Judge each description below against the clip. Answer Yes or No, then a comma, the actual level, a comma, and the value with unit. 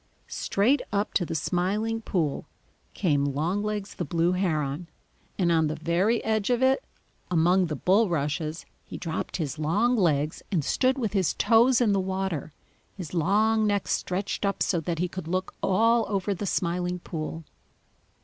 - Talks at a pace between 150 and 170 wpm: Yes, average, 160 wpm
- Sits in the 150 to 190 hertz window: Yes, medium, 185 Hz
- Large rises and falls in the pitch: No, average, 4.2 semitones